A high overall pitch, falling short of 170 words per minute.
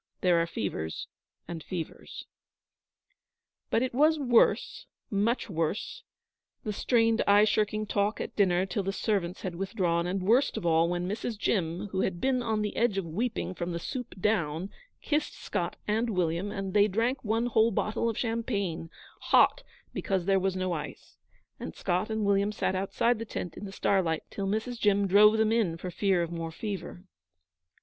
No: high, 200 Hz; average, 175 wpm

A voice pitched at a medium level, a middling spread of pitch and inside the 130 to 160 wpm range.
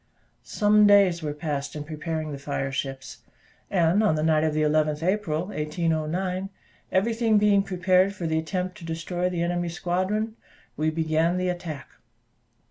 Yes: medium, 170 Hz; average, 3.3 semitones; average, 155 wpm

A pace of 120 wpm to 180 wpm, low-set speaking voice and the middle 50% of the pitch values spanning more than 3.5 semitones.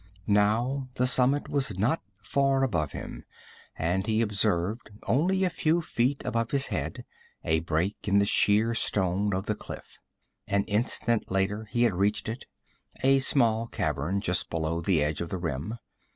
Yes: average, 165 wpm; low, 105 Hz; average, 5.1 semitones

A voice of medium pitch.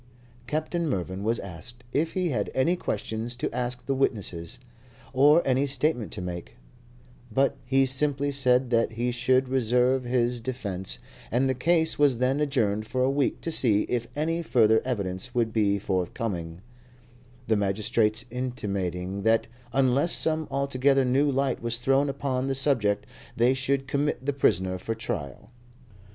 No: low, 125 Hz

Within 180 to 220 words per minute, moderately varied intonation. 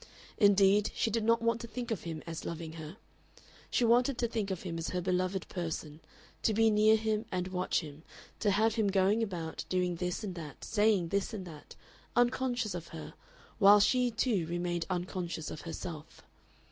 Yes: average, 185 wpm; average, 4.5 semitones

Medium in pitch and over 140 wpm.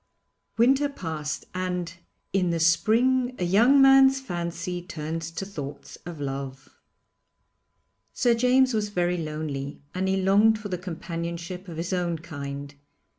No: medium, 180 Hz; slow, 135 wpm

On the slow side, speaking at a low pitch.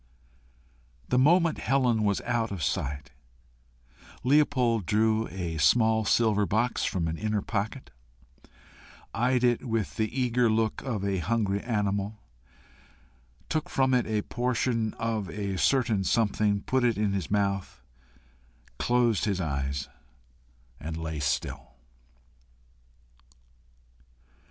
Yes: slow, 115 wpm; low, 110 Hz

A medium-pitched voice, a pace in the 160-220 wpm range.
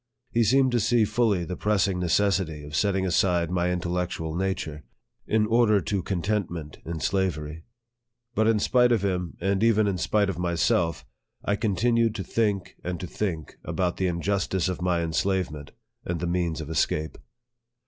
No: very low, 95 Hz; average, 170 wpm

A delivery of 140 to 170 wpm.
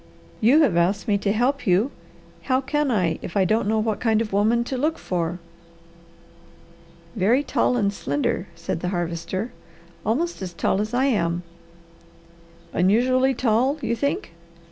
Yes: average, 160 wpm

